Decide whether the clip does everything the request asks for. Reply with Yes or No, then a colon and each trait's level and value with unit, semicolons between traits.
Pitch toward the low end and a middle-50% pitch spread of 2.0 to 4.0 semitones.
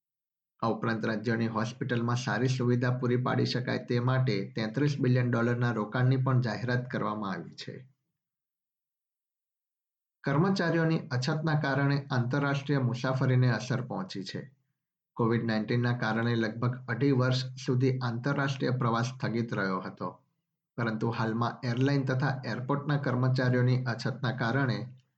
Yes: low, 125 Hz; average, 2.8 semitones